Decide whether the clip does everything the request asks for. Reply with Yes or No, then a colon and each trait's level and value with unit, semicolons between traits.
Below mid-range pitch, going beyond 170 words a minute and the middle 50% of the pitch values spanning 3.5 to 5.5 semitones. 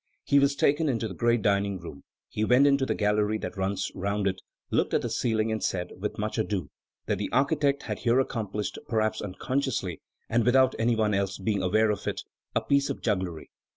Yes: low, 110 Hz; fast, 205 wpm; average, 3.9 semitones